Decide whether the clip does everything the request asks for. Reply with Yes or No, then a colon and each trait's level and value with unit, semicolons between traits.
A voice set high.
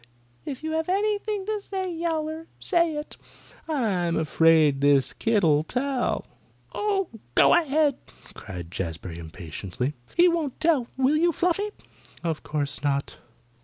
Yes: very high, 275 Hz